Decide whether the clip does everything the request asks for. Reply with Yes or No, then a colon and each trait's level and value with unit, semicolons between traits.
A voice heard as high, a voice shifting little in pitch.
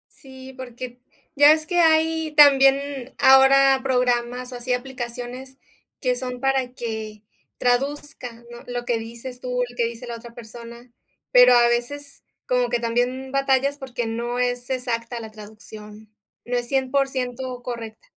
Yes: very high, 250 Hz; narrow, 1.9 semitones